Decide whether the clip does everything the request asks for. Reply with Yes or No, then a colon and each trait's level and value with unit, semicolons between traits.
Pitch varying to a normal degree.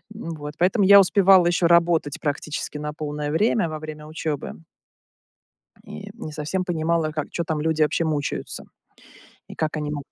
No: narrow, 2.3 semitones